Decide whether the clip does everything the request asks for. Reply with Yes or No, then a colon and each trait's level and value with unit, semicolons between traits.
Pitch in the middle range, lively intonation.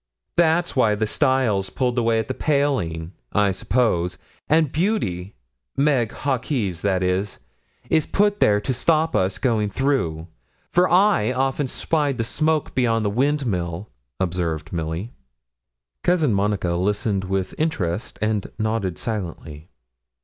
No: low, 110 Hz; wide, 6.8 semitones